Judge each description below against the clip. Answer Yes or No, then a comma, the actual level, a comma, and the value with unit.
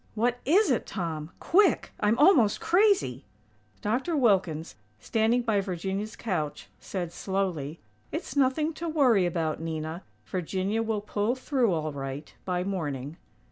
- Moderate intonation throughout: No, wide, 7.0 semitones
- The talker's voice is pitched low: No, high, 200 Hz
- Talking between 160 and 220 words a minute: No, slow, 135 wpm